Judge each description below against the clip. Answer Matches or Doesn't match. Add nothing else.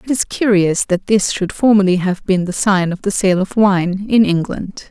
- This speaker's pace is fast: Matches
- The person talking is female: Matches